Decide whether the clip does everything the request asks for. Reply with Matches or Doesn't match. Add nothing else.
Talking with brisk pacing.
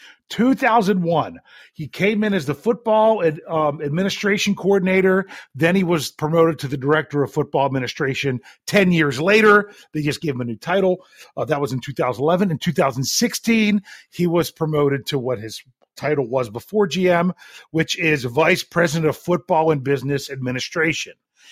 Doesn't match